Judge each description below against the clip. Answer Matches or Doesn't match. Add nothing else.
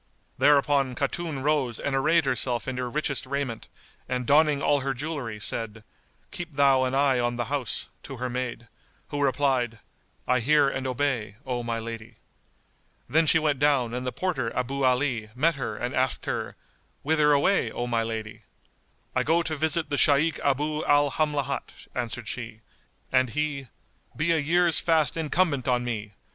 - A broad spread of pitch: Doesn't match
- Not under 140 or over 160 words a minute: Doesn't match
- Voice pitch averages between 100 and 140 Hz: Matches